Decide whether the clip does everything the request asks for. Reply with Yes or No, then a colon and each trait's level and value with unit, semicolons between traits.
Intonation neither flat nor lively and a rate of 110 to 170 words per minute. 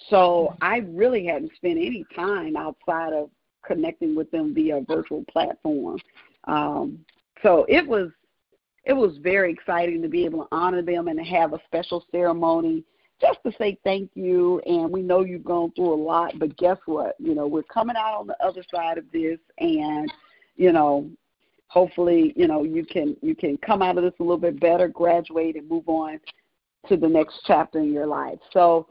No: average, 4.1 semitones; average, 195 wpm